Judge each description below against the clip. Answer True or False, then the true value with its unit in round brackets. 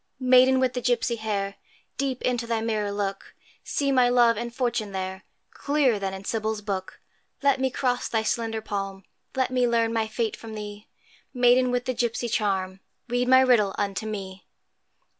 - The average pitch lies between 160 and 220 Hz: False (230 Hz)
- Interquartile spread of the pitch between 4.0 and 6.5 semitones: False (3.3 semitones)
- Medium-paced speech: True (175 wpm)